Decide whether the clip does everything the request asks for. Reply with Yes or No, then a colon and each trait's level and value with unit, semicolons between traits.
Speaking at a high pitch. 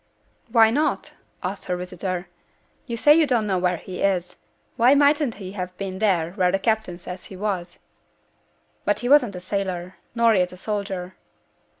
Yes: high, 195 Hz